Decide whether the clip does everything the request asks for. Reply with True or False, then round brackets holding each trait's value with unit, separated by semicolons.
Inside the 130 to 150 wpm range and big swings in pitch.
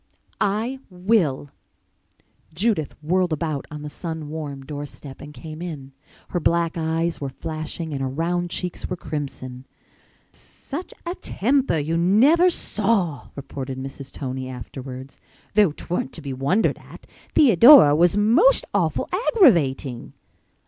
True (135 wpm; 5.7 semitones)